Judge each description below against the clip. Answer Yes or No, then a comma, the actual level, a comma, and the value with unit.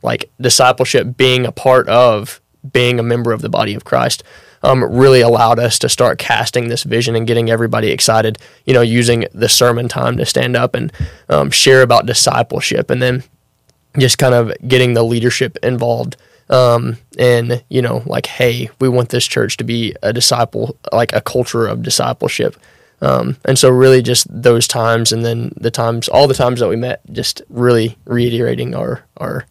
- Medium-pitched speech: No, low, 120 Hz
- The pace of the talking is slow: No, average, 185 wpm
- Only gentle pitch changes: Yes, narrow, 1.5 semitones